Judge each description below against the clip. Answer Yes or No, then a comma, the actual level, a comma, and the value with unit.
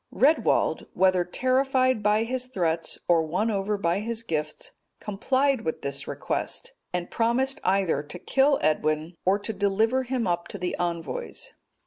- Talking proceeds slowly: No, average, 150 wpm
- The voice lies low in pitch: No, high, 200 Hz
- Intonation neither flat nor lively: No, wide, 6.6 semitones